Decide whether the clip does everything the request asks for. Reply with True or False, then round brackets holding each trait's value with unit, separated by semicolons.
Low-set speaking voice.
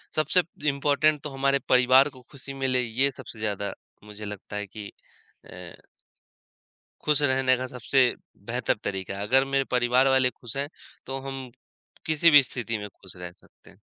True (130 Hz)